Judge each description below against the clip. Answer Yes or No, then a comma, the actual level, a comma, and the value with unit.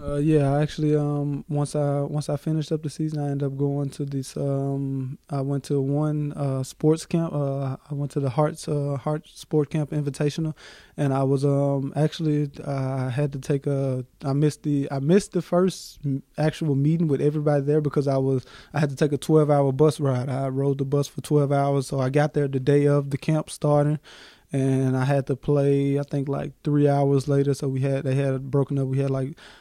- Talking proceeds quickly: Yes, fast, 220 wpm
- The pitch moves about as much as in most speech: No, narrow, 1.5 semitones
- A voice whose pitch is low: No, medium, 145 Hz